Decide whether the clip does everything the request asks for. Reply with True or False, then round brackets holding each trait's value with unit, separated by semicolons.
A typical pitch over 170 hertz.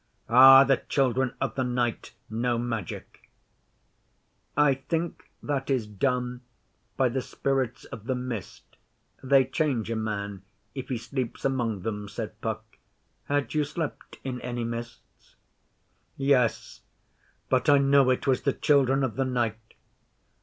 False (125 Hz)